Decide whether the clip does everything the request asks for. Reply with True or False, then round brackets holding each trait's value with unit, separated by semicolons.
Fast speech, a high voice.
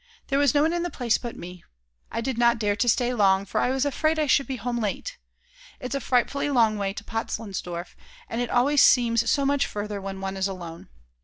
True (230 wpm; 235 Hz)